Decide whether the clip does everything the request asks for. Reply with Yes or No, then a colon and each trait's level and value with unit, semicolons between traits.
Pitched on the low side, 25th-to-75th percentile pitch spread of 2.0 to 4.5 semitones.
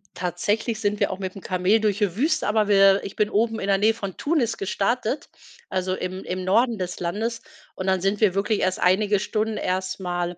No: high, 200 Hz; average, 2.8 semitones